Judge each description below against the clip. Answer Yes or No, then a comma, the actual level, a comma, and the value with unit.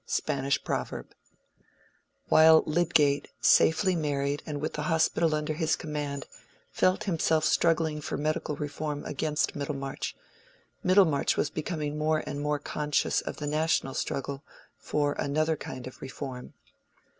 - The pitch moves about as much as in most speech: No, narrow, 1.8 semitones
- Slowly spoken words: Yes, slow, 130 wpm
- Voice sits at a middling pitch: Yes, medium, 150 Hz